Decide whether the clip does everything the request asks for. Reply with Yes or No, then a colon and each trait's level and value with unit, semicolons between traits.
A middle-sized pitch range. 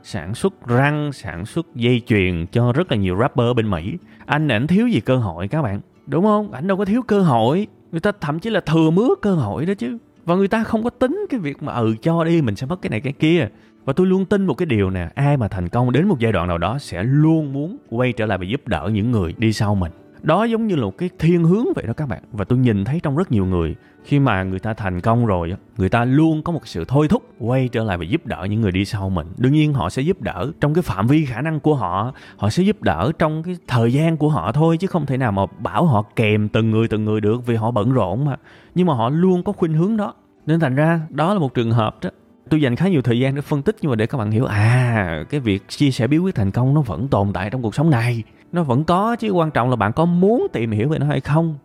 No: wide, 7.2 semitones